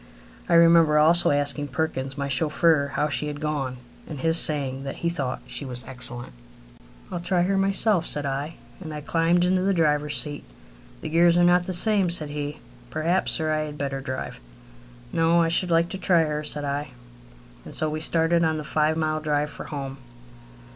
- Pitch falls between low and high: Yes, medium, 155 Hz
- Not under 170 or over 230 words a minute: Yes, average, 195 wpm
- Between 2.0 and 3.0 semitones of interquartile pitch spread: Yes, average, 2.7 semitones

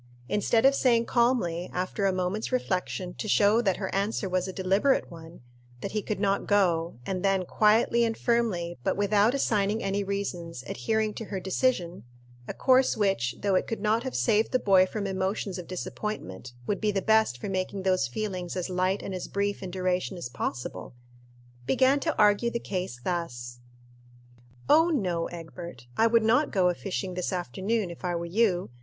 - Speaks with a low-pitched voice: No, high, 195 Hz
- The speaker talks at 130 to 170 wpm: No, average, 185 wpm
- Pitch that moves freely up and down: No, average, 3.4 semitones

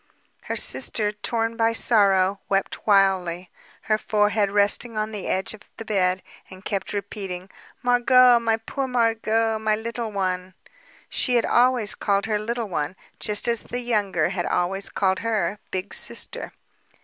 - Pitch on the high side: Yes, high, 210 Hz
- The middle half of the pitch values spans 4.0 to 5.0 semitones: No, average, 2.9 semitones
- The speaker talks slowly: No, average, 150 wpm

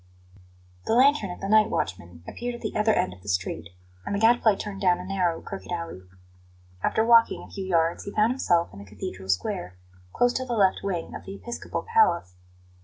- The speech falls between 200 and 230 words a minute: Yes, fast, 205 wpm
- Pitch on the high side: Yes, high, 195 Hz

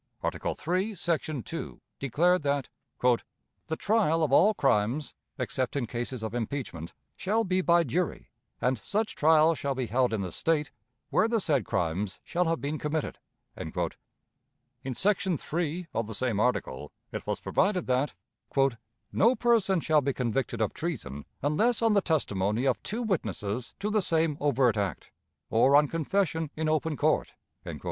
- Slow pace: No, average, 155 wpm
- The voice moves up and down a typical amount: No, wide, 6.5 semitones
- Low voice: No, medium, 150 Hz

